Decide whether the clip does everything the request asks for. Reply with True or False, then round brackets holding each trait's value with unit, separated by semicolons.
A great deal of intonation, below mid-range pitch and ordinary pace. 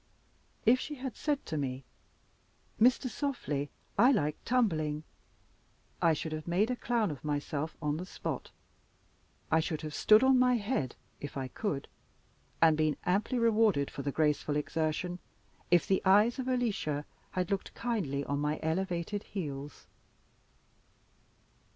False (7.3 semitones; 170 Hz; 145 wpm)